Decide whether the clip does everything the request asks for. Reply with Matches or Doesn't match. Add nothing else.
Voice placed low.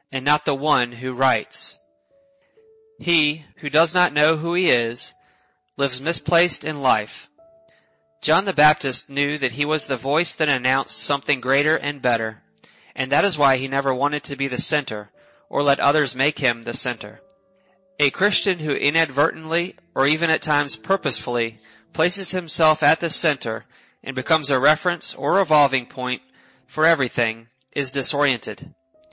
Doesn't match